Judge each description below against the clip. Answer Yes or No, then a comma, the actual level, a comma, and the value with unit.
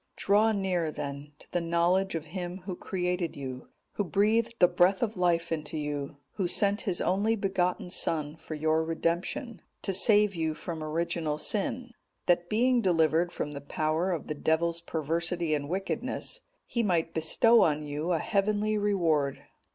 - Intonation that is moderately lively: Yes, average, 3.9 semitones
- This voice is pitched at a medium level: Yes, medium, 175 Hz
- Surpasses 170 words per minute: No, average, 165 wpm